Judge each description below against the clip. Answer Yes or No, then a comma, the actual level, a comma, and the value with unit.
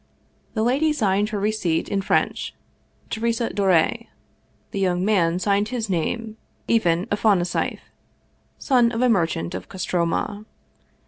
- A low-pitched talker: No, high, 205 Hz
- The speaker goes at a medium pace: No, slow, 125 wpm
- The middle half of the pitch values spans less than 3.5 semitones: No, average, 4.2 semitones